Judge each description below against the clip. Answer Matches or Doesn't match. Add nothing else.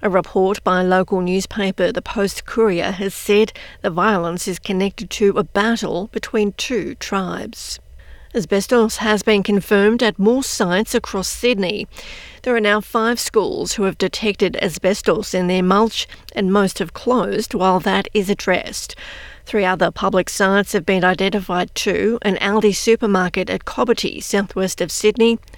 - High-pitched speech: Matches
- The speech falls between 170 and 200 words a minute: Doesn't match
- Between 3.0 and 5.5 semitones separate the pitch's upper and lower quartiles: Doesn't match